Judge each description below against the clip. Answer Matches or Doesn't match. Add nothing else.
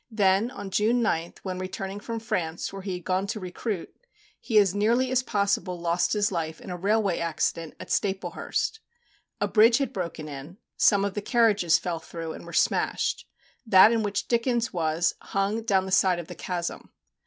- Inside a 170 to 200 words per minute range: Matches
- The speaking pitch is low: Doesn't match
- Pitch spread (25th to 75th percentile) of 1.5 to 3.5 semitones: Doesn't match